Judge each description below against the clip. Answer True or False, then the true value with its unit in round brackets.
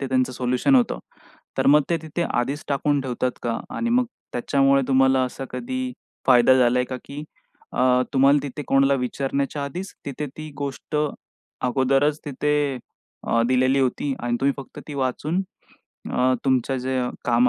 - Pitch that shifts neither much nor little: False (2.3 semitones)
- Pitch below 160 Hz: True (135 Hz)